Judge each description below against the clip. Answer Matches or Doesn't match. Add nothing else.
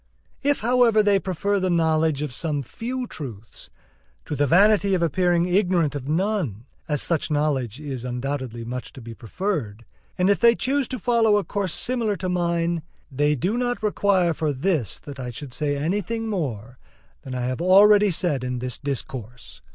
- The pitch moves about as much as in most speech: Doesn't match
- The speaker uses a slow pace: Doesn't match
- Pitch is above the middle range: Doesn't match